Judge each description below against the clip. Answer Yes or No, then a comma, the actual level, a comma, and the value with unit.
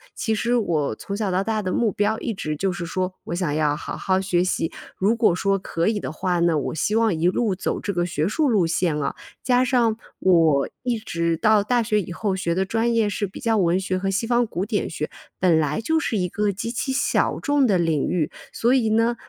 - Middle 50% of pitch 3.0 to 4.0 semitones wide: No, average, 4.6 semitones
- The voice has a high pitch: Yes, high, 195 Hz